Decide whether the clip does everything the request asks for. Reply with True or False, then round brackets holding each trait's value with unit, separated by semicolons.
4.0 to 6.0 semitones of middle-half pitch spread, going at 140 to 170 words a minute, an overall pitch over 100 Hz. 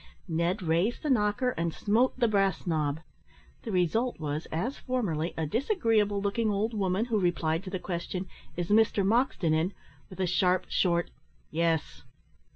True (4.6 semitones; 160 wpm; 190 Hz)